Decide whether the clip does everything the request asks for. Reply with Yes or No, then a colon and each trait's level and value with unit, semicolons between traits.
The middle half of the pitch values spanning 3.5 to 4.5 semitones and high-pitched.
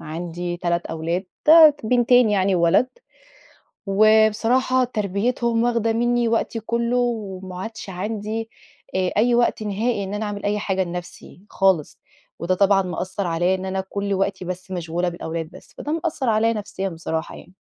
Yes: average, 4.1 semitones; high, 200 Hz